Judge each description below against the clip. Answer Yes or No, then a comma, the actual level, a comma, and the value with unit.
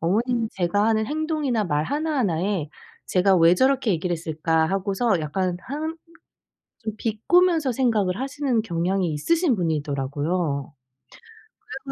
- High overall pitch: Yes, high, 200 Hz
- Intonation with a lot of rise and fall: Yes, wide, 7.8 semitones